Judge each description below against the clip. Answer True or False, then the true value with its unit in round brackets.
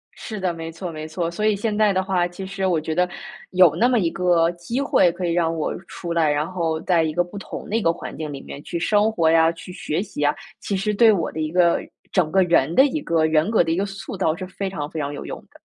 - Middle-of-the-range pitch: True (175 Hz)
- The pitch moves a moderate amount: True (3.1 semitones)